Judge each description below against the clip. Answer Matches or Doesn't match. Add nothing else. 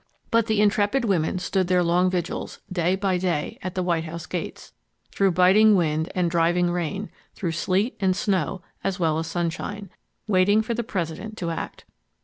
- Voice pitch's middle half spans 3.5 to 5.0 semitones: Doesn't match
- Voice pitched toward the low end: Doesn't match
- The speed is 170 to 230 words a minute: Matches